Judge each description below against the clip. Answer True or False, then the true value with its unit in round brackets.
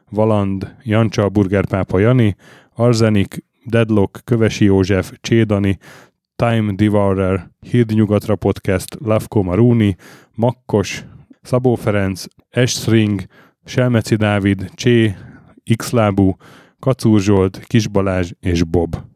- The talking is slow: True (90 wpm)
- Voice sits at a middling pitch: False (105 Hz)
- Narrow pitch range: False (3.1 semitones)